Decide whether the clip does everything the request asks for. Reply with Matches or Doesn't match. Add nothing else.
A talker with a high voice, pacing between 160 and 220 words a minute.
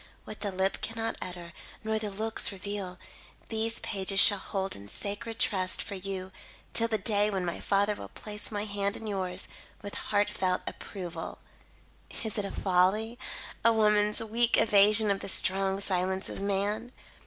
Matches